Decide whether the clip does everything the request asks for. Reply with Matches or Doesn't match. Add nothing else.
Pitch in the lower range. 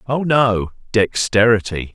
Matches